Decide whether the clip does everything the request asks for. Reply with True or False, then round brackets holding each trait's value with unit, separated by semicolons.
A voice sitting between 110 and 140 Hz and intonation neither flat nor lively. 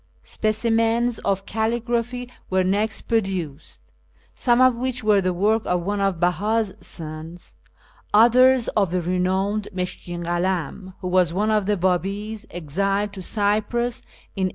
False (200 Hz; 3.5 semitones)